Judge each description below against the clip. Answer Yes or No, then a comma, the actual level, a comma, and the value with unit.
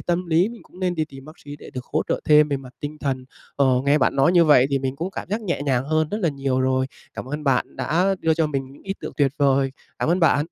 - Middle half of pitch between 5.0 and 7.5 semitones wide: No, average, 3.6 semitones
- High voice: No, medium, 150 Hz